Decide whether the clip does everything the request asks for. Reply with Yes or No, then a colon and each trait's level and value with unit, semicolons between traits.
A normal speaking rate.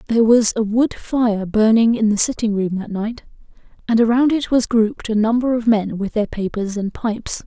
No: fast, 210 wpm